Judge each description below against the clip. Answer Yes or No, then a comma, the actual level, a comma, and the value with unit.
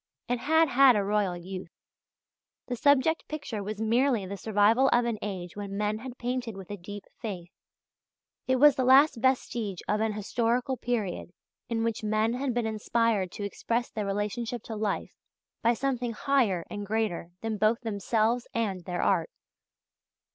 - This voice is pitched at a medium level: No, high, 225 Hz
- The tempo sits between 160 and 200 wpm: Yes, average, 165 wpm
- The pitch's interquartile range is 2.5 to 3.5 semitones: Yes, average, 3.2 semitones